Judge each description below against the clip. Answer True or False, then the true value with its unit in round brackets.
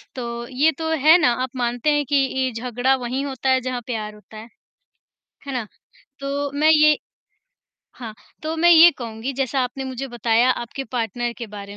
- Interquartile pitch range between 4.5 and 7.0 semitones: False (2.8 semitones)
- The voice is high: True (255 Hz)